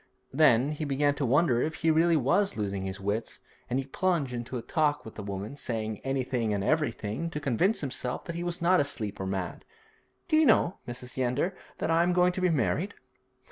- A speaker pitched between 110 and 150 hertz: Yes, medium, 140 Hz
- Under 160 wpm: No, fast, 205 wpm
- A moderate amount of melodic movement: No, wide, 6.3 semitones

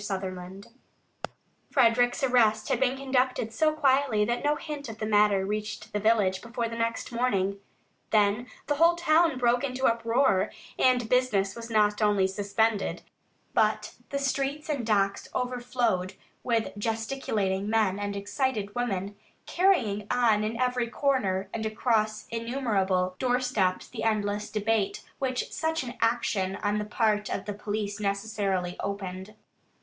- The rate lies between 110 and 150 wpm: Yes, average, 140 wpm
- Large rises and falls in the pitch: No, average, 3.7 semitones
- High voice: Yes, high, 220 Hz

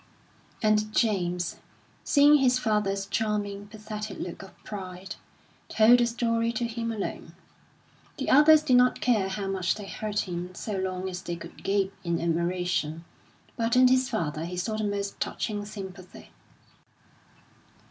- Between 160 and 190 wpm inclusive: No, average, 145 wpm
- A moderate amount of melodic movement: Yes, average, 3.9 semitones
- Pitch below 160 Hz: No, high, 205 Hz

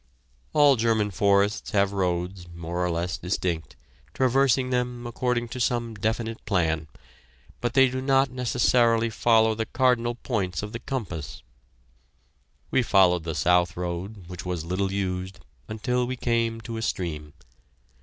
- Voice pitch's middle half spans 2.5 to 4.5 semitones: No, average, 5.1 semitones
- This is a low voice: Yes, low, 110 Hz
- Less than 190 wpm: Yes, average, 145 wpm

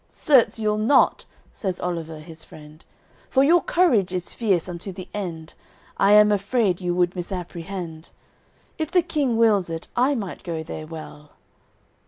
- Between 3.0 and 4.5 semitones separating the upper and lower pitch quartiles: No, average, 5.0 semitones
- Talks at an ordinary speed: Yes, average, 155 wpm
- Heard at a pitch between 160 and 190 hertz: Yes, medium, 185 Hz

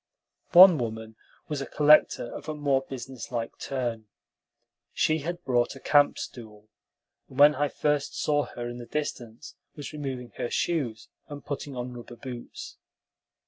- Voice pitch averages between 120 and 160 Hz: Yes, low, 135 Hz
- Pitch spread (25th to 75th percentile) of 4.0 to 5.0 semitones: No, average, 3.5 semitones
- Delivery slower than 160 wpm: Yes, average, 150 wpm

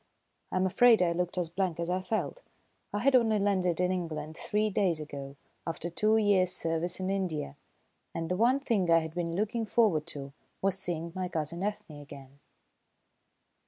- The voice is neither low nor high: Yes, medium, 180 Hz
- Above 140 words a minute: Yes, average, 180 wpm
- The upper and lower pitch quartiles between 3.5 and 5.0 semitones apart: Yes, average, 3.8 semitones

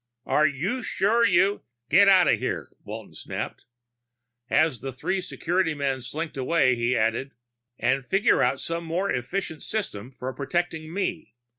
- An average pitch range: No, wide, 6.2 semitones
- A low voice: No, medium, 160 Hz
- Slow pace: No, average, 155 wpm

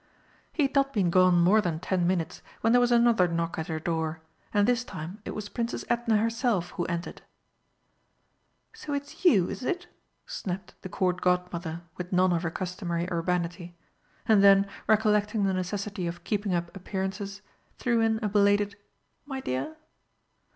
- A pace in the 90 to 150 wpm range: No, average, 165 wpm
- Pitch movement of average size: Yes, average, 4.0 semitones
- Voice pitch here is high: Yes, high, 195 Hz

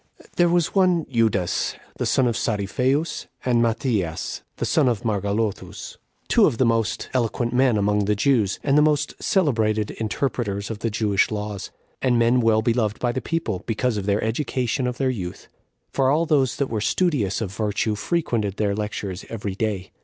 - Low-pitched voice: Yes, low, 115 Hz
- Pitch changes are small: No, average, 3.9 semitones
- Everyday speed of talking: Yes, average, 180 wpm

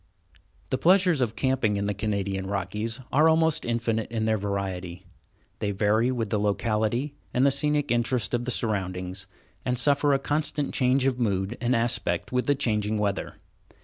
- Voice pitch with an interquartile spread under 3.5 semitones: No, average, 4.3 semitones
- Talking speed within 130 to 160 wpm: No, average, 170 wpm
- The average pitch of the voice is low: Yes, low, 115 Hz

